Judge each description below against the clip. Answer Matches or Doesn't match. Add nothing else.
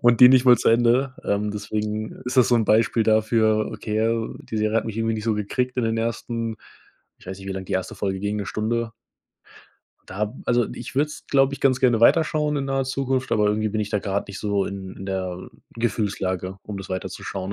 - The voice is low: Matches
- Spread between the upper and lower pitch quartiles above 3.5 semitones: Doesn't match